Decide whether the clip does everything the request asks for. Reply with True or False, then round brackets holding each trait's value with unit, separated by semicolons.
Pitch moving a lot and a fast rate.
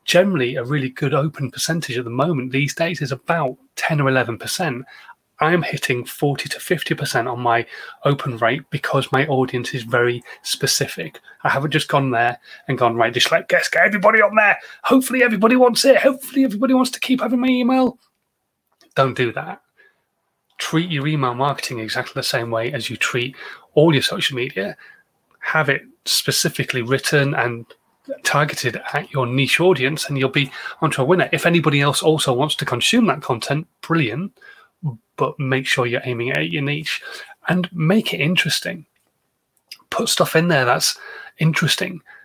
False (5.7 semitones; 170 wpm)